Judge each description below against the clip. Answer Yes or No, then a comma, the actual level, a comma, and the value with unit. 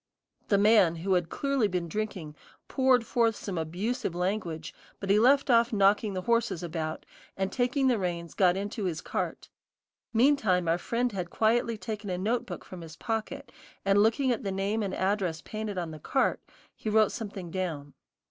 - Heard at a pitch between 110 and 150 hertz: No, high, 200 Hz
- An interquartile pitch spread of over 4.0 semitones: Yes, average, 4.4 semitones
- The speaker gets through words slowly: No, average, 175 wpm